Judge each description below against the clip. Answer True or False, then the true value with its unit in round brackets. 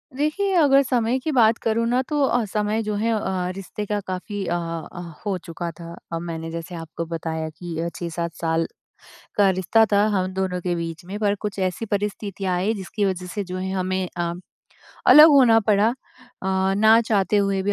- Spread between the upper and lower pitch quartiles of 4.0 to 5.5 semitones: True (4.3 semitones)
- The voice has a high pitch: True (195 Hz)